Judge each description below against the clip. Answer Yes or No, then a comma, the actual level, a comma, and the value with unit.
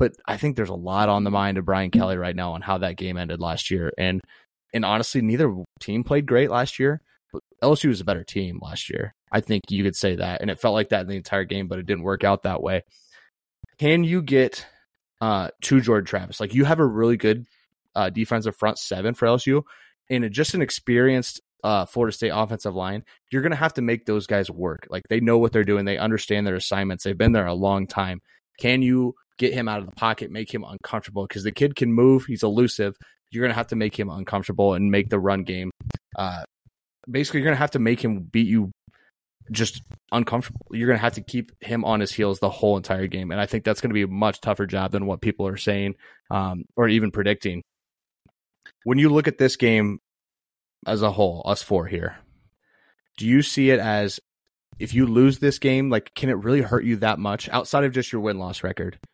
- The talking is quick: Yes, fast, 230 wpm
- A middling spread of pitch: Yes, average, 3.8 semitones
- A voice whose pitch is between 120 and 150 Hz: No, low, 110 Hz